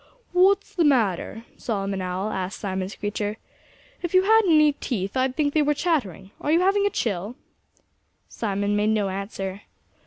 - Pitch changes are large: Yes, wide, 7.8 semitones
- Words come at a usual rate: Yes, average, 160 wpm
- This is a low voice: No, high, 220 Hz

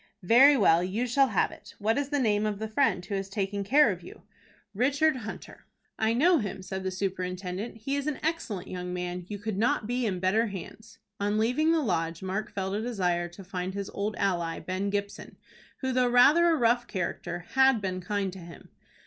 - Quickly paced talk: Yes, fast, 210 wpm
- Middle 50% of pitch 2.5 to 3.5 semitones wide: No, average, 4.8 semitones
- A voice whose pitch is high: Yes, high, 205 Hz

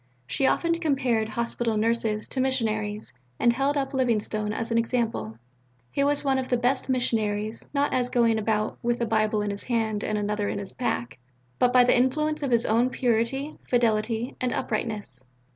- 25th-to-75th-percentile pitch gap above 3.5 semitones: No, average, 3.0 semitones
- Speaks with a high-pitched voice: Yes, high, 235 Hz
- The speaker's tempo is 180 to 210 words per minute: Yes, average, 185 wpm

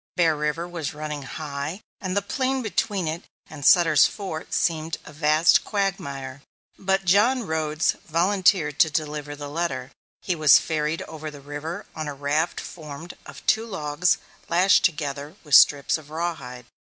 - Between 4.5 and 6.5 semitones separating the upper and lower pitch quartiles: No, average, 3.2 semitones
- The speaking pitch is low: No, medium, 155 Hz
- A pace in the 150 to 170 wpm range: Yes, average, 155 wpm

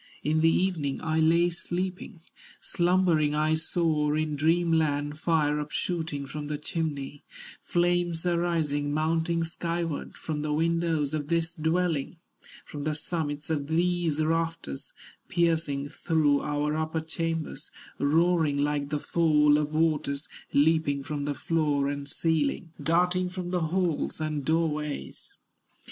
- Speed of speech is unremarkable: No, slow, 130 wpm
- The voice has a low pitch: No, medium, 160 Hz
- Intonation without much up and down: Yes, narrow, 2.2 semitones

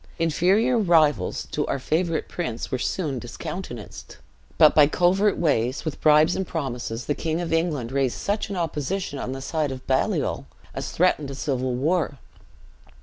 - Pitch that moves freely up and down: No, average, 4.8 semitones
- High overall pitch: No, medium, 155 Hz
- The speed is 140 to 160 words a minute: No, average, 175 wpm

